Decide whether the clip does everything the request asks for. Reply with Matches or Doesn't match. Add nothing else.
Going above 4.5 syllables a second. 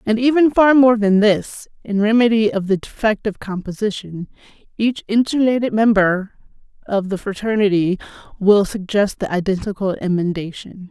Matches